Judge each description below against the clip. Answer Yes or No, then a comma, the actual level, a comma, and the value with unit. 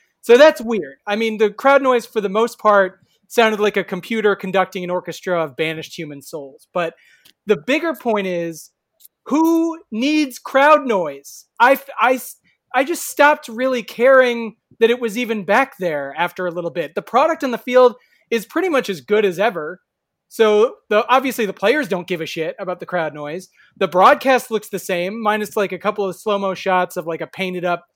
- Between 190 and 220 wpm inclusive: Yes, average, 195 wpm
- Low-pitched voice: No, high, 210 Hz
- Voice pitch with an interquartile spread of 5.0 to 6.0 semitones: Yes, wide, 5.5 semitones